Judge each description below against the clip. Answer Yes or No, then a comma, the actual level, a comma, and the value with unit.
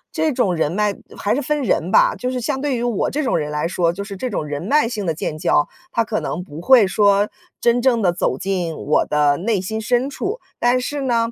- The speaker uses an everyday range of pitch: No, wide, 6.3 semitones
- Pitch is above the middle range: Yes, high, 215 Hz